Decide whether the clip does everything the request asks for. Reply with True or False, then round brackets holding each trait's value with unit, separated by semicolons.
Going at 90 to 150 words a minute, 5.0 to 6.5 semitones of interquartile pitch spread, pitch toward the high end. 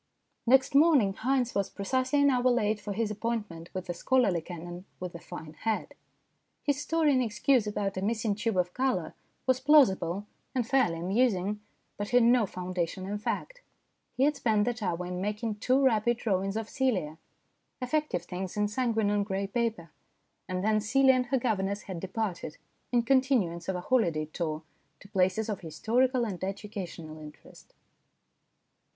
False (165 wpm; 5.3 semitones; 210 Hz)